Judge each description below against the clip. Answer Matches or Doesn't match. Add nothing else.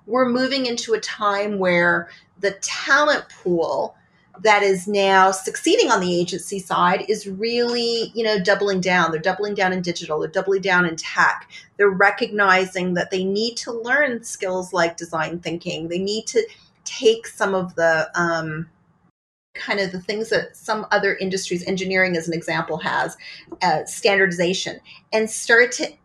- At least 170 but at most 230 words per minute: Doesn't match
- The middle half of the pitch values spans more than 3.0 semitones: Matches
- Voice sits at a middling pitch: Doesn't match